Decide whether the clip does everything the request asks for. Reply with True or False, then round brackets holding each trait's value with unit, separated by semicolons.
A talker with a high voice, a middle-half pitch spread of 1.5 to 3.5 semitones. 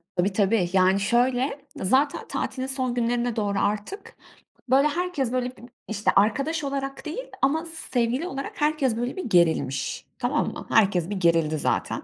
False (245 Hz; 5.6 semitones)